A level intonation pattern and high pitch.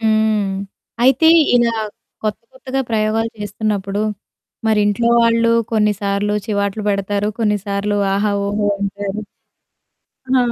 Yes: narrow, 1.6 semitones; high, 210 Hz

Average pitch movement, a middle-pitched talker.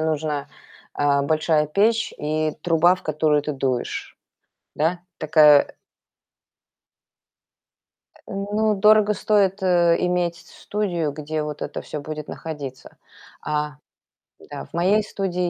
Yes: average, 4.0 semitones; medium, 160 Hz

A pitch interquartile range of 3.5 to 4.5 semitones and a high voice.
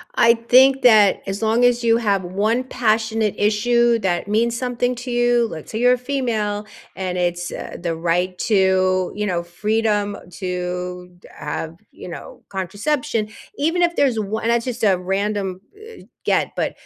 Yes: average, 4.2 semitones; high, 215 Hz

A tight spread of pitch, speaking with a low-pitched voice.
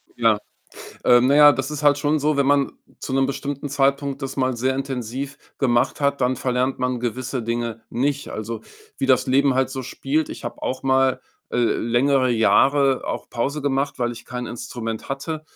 Yes: narrow, 2.3 semitones; low, 130 Hz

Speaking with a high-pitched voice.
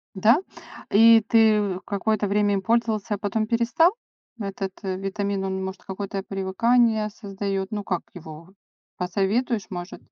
Yes: high, 200 Hz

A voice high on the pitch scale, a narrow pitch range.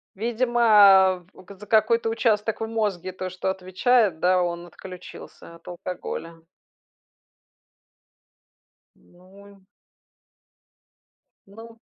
No: high, 195 Hz; average, 3.4 semitones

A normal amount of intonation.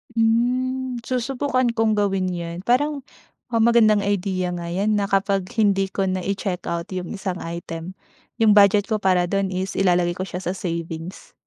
Yes: average, 3.7 semitones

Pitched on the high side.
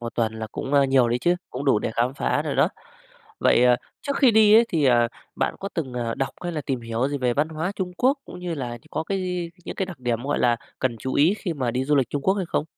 No: medium, 140 Hz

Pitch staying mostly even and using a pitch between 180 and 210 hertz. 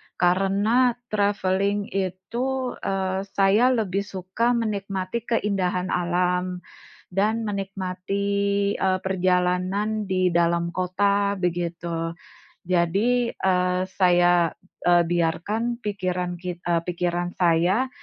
Yes: narrow, 2.2 semitones; medium, 185 Hz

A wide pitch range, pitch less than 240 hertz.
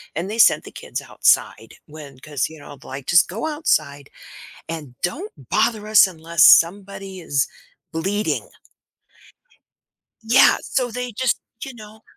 Yes: wide, 6.3 semitones; high, 190 Hz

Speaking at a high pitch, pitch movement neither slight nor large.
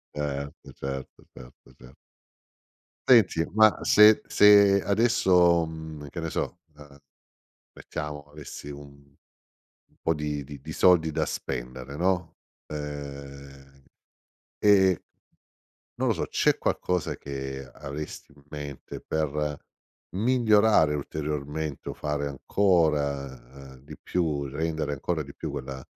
No: very low, 75 Hz; average, 3.4 semitones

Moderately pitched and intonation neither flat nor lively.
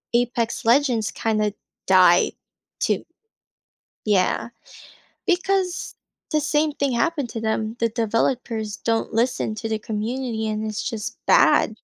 No: high, 225 Hz; average, 3.1 semitones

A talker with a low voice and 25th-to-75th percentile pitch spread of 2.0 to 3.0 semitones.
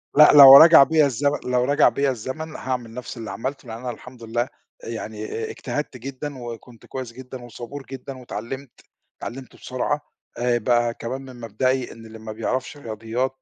Yes: low, 125 Hz; narrow, 2.5 semitones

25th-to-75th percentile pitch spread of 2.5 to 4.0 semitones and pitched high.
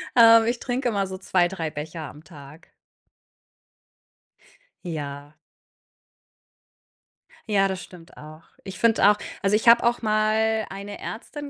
No: wide, 5.4 semitones; high, 195 Hz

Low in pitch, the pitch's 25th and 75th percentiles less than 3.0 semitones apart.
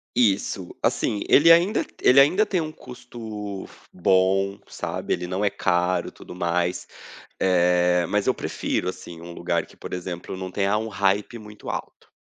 No: very low, 95 Hz; average, 3.7 semitones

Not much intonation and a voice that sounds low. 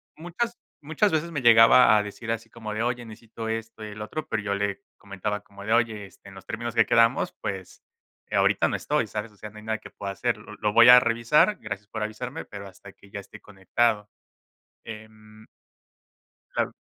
Yes: narrow, 2.3 semitones; low, 110 Hz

